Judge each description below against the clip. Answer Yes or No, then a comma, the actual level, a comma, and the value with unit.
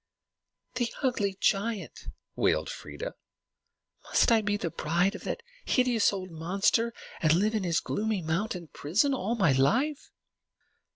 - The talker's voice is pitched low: No, high, 205 Hz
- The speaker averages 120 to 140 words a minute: Yes, slow, 135 wpm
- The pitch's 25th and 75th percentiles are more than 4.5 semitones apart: Yes, average, 5.0 semitones